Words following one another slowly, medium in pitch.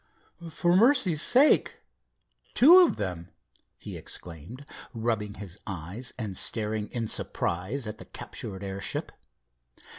No: slow, 115 wpm; low, 110 Hz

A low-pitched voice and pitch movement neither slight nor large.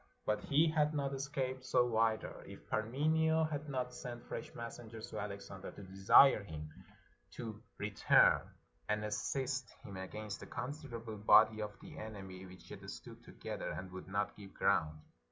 Yes: low, 110 Hz; average, 5.0 semitones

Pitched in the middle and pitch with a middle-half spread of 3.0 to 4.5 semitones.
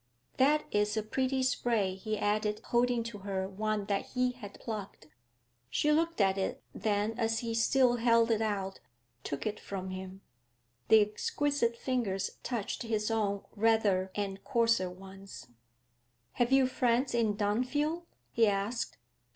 No: high, 220 Hz; average, 3.4 semitones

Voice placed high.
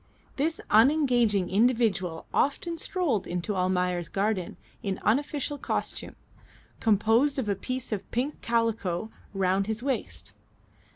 Yes: high, 220 Hz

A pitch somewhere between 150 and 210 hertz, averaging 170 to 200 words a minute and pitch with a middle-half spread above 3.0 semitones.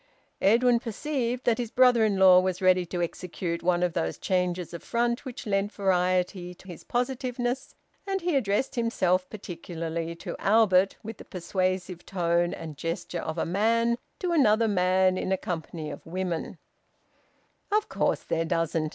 No: medium, 185 Hz; average, 160 wpm; average, 5.0 semitones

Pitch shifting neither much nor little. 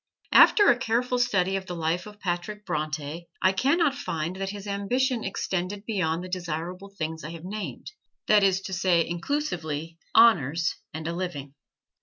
Yes: average, 3.9 semitones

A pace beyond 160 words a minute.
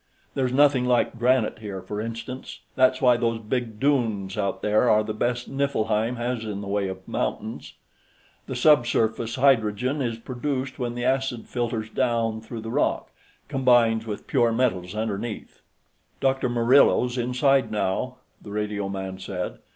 No: average, 150 wpm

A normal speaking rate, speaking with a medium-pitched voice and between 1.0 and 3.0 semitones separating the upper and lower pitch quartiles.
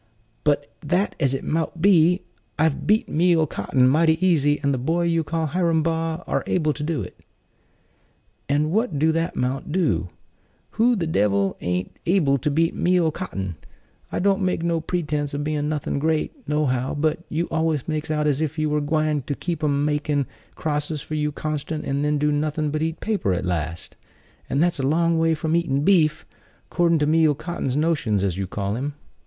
Yes: average, 195 wpm; medium, 155 Hz; narrow, 2.5 semitones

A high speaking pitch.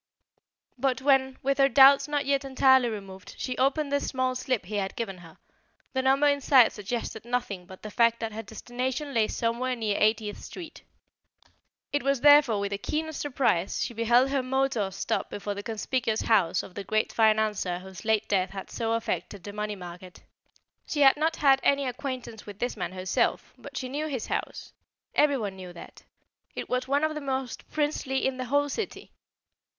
Yes: high, 245 Hz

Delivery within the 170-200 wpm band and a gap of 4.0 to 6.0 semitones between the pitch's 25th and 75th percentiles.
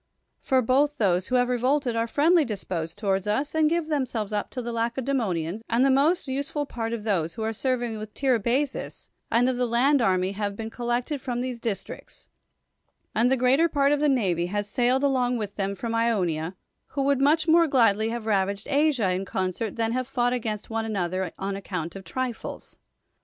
Yes: average, 195 wpm; average, 4.6 semitones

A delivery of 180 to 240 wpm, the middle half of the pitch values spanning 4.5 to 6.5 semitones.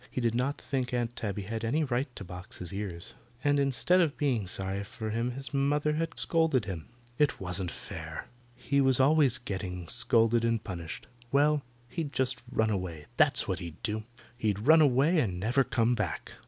Yes: average, 185 wpm; wide, 5.6 semitones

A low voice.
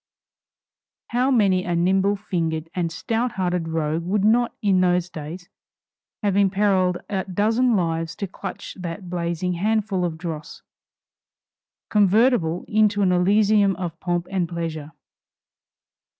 No: medium, 185 Hz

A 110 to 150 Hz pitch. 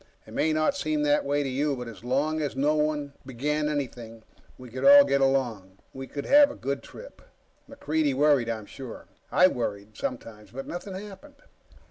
Yes: medium, 140 Hz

